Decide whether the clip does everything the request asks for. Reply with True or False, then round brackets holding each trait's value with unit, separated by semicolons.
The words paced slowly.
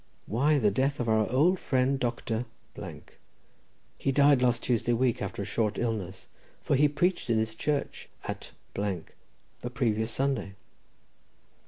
False (145 wpm)